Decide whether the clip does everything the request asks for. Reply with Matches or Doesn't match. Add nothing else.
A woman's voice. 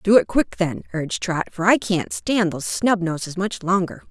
Matches